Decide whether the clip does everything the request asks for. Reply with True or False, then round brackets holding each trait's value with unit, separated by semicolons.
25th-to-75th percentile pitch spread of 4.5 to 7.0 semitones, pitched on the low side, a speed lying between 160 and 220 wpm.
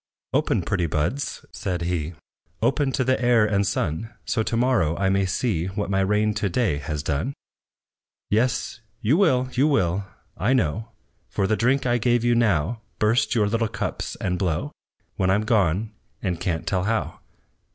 True (4.9 semitones; 105 Hz; 170 wpm)